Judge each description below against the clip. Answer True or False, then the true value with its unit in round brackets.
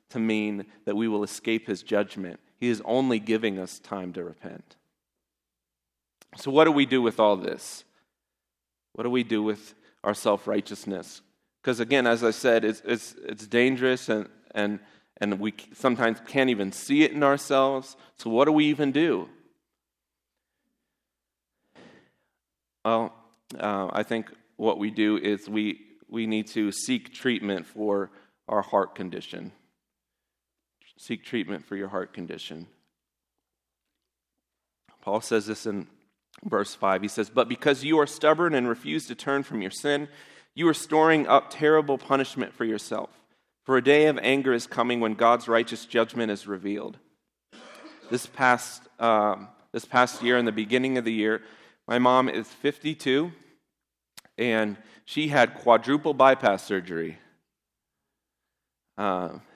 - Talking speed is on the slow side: False (145 wpm)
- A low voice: True (115 Hz)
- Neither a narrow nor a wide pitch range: True (4.0 semitones)